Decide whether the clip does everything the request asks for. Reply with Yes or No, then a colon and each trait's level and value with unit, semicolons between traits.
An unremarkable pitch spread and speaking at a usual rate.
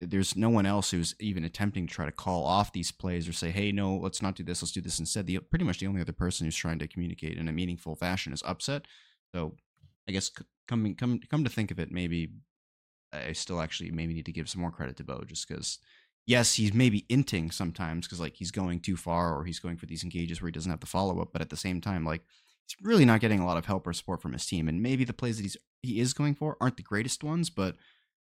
No: average, 3.7 semitones; fast, 270 wpm